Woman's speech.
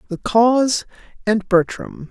Yes: female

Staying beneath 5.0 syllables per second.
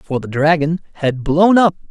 Yes: 4.4 syllables/s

